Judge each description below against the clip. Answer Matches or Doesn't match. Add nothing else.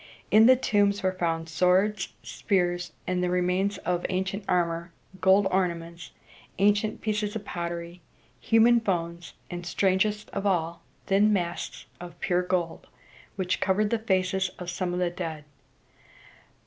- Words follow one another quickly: Doesn't match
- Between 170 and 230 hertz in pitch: Matches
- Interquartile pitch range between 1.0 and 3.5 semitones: Matches